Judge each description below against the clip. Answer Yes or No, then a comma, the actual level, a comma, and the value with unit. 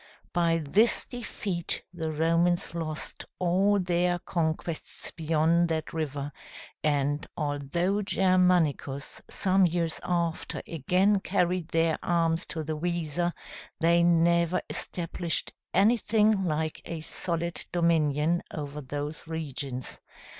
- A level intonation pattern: Yes, narrow, 2.2 semitones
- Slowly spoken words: Yes, slow, 105 wpm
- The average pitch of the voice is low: No, medium, 170 Hz